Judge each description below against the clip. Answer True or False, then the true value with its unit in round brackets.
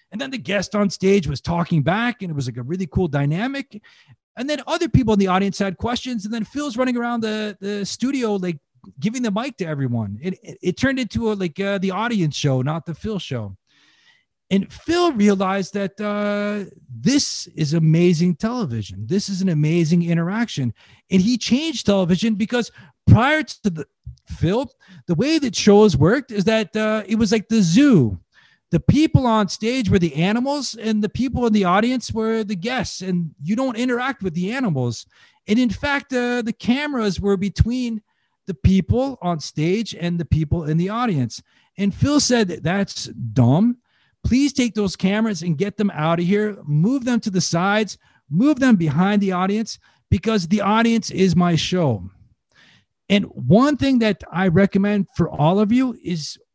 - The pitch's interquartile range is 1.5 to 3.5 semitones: False (5.1 semitones)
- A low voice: False (200 Hz)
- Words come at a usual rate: False (185 wpm)